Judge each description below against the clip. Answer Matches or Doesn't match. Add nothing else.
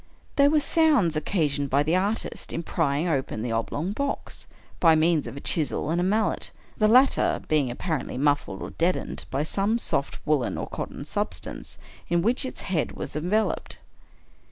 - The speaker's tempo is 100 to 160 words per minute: Doesn't match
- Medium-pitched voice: Matches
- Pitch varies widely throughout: Matches